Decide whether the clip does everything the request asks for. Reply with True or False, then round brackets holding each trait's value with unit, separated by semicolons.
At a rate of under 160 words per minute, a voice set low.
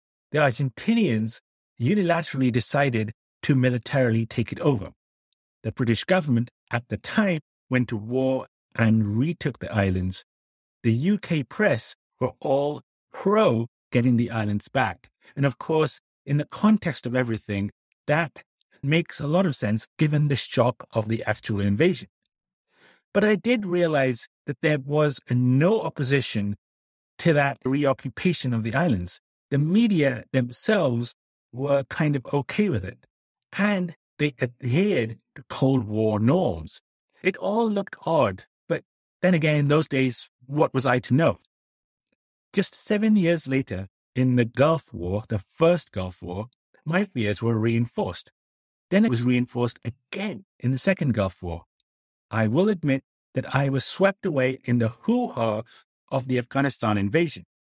True (145 wpm; 130 Hz)